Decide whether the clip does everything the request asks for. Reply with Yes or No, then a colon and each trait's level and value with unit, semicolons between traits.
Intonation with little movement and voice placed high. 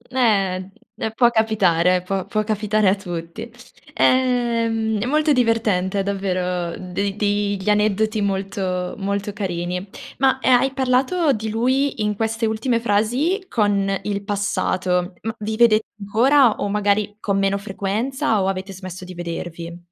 No: average, 3.0 semitones; high, 205 Hz